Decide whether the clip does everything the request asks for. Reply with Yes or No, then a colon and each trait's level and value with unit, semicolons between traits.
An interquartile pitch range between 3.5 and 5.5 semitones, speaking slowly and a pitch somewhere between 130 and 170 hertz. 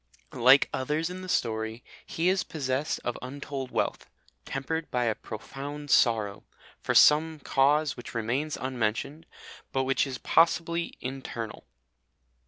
Yes: average, 3.9 semitones; slow, 130 wpm; low, 135 Hz